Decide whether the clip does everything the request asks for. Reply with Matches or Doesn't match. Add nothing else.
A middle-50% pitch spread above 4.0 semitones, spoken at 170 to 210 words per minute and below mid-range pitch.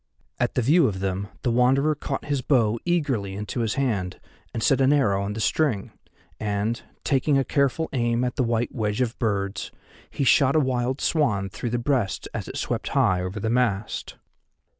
Matches